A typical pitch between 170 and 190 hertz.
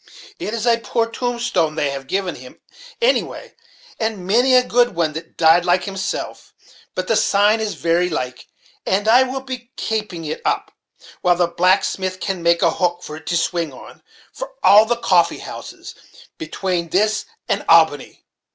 Yes: medium, 185 Hz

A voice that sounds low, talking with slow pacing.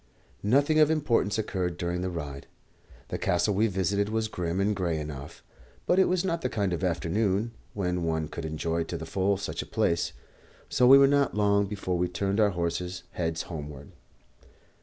No: very low, 95 Hz; average, 185 wpm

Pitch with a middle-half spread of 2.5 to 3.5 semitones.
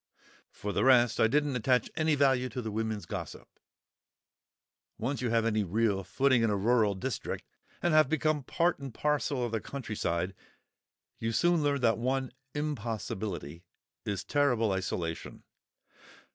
No: average, 4.6 semitones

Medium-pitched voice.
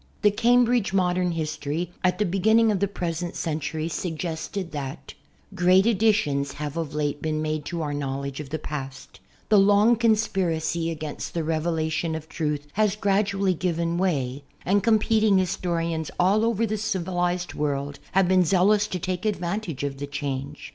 Yes: medium, 175 Hz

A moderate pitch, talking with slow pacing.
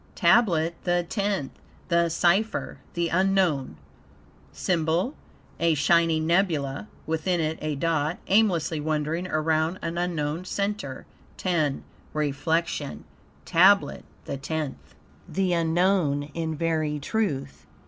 Yes: medium, 165 Hz; slow, 105 wpm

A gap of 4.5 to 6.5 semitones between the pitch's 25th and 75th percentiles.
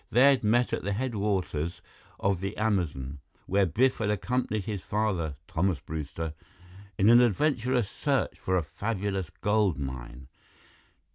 Yes: average, 5.1 semitones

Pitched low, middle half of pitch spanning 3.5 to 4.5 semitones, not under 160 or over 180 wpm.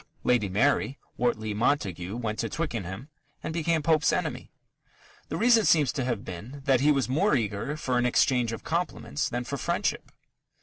No: low, 125 Hz; average, 5.0 semitones; average, 170 wpm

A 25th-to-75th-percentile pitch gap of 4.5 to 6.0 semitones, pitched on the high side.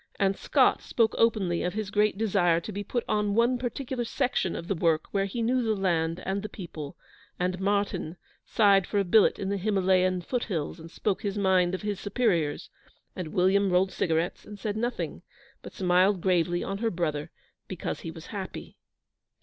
No: average, 3.0 semitones; high, 195 Hz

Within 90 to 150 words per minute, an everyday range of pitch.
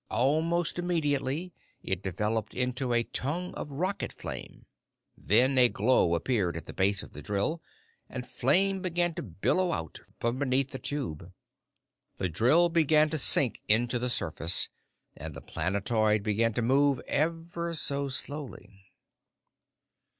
No: average, 140 wpm; wide, 7.0 semitones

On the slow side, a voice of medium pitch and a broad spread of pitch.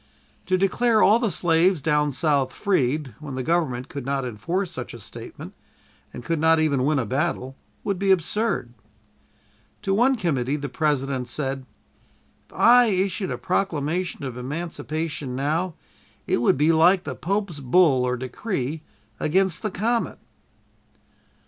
No: average, 150 wpm; medium, 155 Hz; wide, 5.7 semitones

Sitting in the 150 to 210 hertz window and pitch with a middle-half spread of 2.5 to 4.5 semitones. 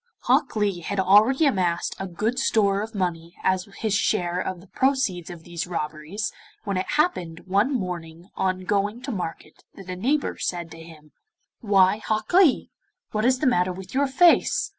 Yes: high, 190 Hz; average, 4.0 semitones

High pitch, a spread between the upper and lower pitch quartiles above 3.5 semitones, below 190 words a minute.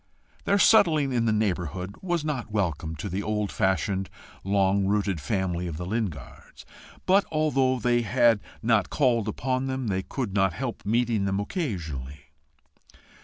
No: low, 105 Hz; average, 5.2 semitones; average, 150 wpm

